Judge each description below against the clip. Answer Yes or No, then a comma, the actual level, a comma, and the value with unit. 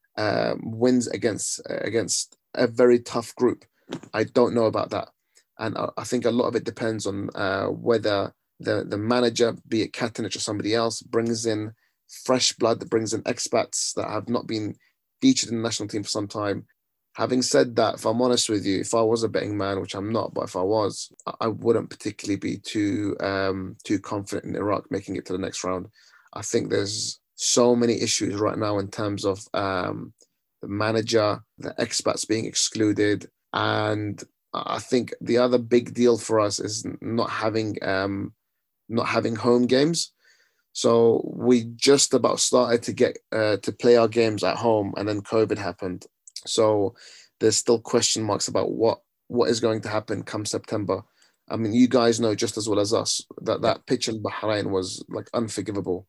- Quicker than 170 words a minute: Yes, average, 190 wpm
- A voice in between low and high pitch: No, low, 110 Hz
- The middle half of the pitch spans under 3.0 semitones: Yes, narrow, 2.4 semitones